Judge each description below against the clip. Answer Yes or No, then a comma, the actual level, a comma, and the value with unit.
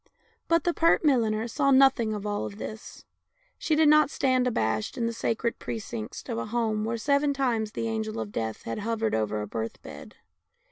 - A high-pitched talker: Yes, high, 225 Hz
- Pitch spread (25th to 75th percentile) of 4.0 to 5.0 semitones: Yes, average, 4.5 semitones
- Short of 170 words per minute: No, average, 190 wpm